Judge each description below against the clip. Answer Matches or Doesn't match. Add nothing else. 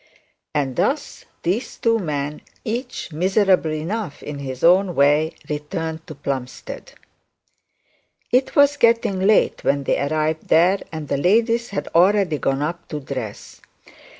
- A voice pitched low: Doesn't match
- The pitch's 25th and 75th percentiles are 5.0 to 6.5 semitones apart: Matches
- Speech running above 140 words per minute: Doesn't match